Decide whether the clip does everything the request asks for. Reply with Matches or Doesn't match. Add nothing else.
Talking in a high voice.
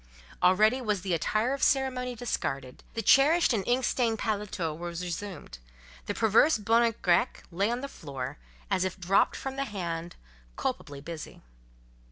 Matches